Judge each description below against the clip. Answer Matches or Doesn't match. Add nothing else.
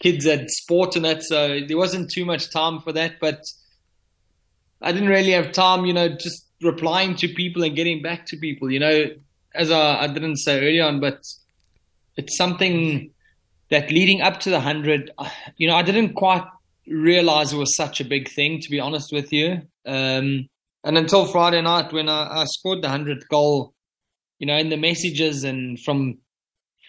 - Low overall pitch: Doesn't match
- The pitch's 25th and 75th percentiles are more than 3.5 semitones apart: Doesn't match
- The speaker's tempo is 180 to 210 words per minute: Matches